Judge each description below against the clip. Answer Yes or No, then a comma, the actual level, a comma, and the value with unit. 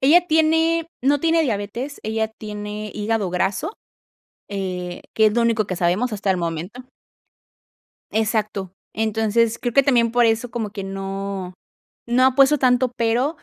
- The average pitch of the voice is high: Yes, high, 220 Hz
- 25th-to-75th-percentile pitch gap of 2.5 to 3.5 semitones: No, average, 4.1 semitones